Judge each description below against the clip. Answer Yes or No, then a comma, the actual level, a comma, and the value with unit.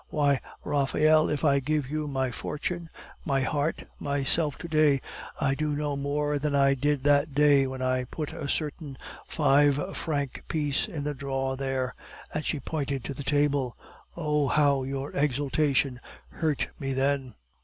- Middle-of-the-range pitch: Yes, medium, 145 Hz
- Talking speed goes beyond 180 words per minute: No, average, 160 wpm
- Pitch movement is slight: Yes, narrow, 1.7 semitones